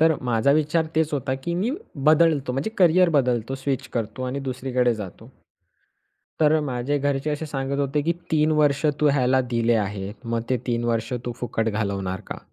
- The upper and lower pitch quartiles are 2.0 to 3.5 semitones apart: No, average, 4.1 semitones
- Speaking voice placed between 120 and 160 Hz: Yes, low, 135 Hz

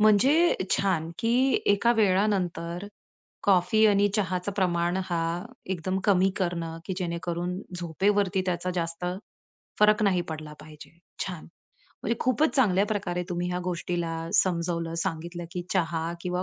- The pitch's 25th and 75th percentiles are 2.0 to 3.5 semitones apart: Yes, average, 2.9 semitones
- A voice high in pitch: No, medium, 180 Hz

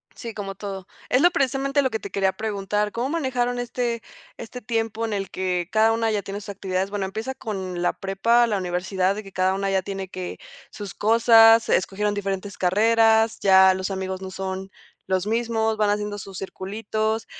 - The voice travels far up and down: No, average, 2.8 semitones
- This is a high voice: Yes, high, 205 Hz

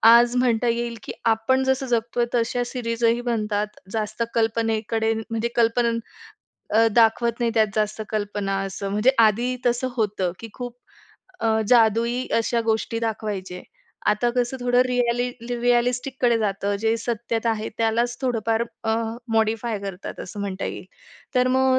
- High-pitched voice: Yes, high, 230 Hz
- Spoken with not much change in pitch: Yes, narrow, 1.8 semitones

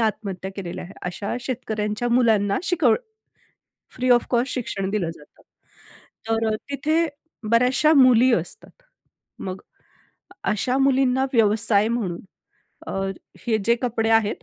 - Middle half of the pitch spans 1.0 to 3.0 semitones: No, average, 3.7 semitones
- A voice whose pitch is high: Yes, high, 230 Hz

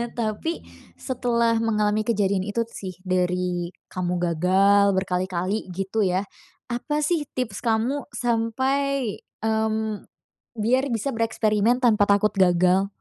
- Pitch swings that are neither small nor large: Yes, average, 3.7 semitones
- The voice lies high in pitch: Yes, high, 215 Hz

